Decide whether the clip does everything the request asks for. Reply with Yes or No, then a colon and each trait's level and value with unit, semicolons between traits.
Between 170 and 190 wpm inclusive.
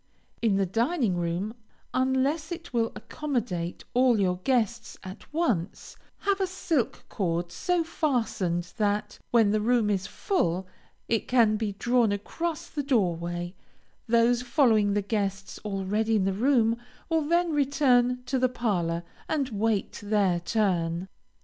No: average, 145 wpm